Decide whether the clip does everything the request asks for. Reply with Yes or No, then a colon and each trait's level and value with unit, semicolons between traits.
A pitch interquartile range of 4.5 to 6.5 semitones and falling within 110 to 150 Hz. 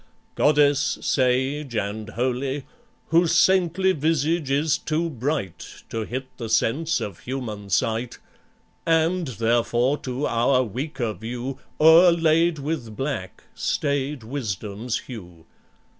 Yes: average, 5.2 semitones; low, 135 Hz